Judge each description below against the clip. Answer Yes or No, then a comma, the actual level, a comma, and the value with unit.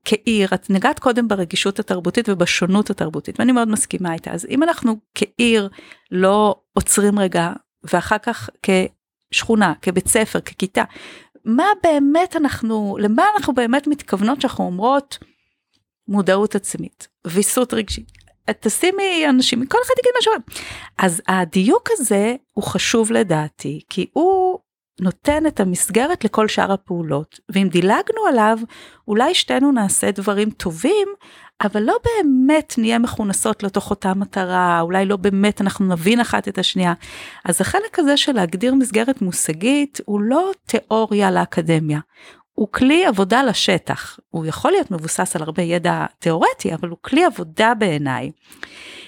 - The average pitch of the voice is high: Yes, high, 215 Hz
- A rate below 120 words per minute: No, average, 135 wpm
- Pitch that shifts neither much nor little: No, wide, 6.2 semitones